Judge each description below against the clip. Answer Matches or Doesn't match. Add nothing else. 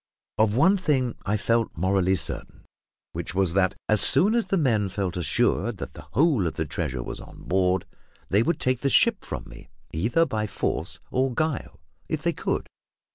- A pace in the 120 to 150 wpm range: Doesn't match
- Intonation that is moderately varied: Doesn't match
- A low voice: Matches